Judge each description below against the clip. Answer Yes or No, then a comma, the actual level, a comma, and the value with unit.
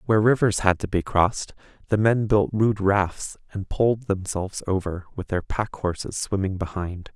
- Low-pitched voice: Yes, low, 100 Hz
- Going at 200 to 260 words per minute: No, average, 175 wpm